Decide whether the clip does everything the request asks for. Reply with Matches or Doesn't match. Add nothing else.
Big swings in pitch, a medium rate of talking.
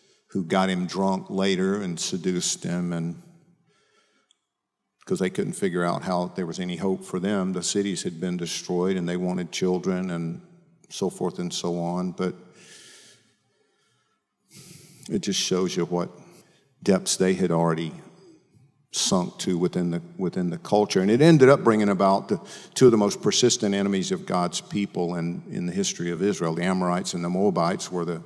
Matches